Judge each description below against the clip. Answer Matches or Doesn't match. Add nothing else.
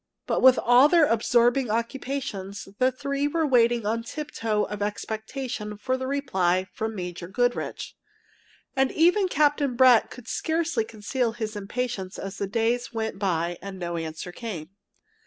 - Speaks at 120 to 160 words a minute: Matches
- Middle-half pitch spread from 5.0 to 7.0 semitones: Doesn't match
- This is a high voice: Matches